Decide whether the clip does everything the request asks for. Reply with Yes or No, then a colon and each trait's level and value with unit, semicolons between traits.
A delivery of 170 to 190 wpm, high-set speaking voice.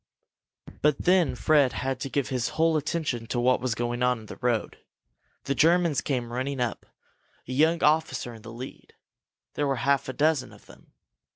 No: average, 185 wpm; low, 135 Hz